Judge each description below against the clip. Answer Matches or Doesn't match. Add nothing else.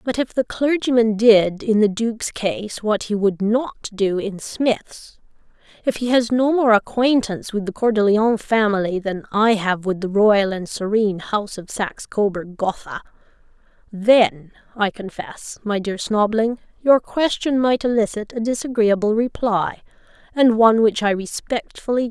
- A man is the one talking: Doesn't match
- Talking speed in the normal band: Matches